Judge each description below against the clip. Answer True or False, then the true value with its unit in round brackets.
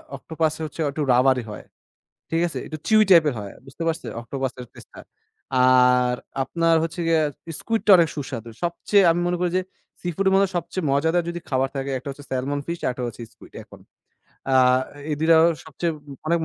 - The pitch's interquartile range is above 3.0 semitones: True (4.7 semitones)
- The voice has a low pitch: False (155 Hz)